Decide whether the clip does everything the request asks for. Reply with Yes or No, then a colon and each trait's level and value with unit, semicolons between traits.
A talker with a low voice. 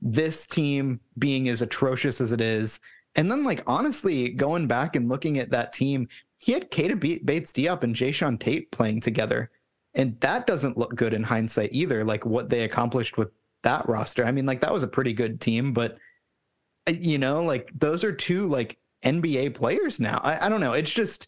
Yes: low, 130 Hz